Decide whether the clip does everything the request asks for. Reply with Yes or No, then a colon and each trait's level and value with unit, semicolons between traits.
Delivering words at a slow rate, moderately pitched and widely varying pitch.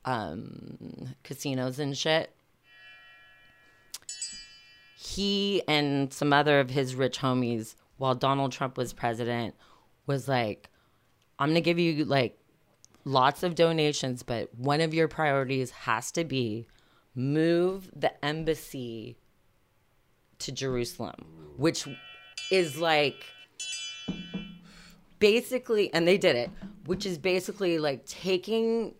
Yes: slow, 110 wpm; medium, 145 Hz; wide, 6.1 semitones